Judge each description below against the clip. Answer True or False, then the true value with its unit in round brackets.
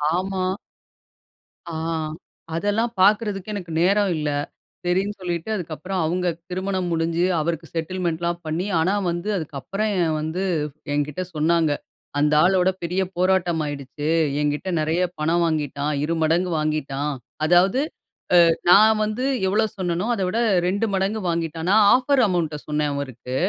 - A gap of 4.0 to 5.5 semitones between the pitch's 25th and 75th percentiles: False (3.6 semitones)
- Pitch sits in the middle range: True (175 Hz)